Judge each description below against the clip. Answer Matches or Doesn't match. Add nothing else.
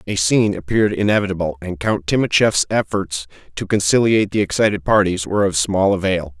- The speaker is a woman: Doesn't match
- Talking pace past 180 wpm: Doesn't match